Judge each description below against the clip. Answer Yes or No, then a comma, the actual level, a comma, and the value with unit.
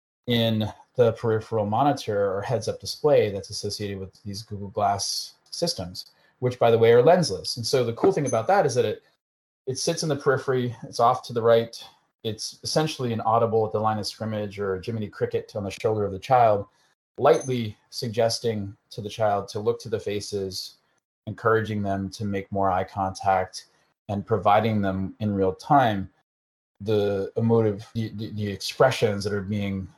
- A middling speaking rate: Yes, average, 180 wpm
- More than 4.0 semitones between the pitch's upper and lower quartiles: No, average, 2.9 semitones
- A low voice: Yes, low, 110 Hz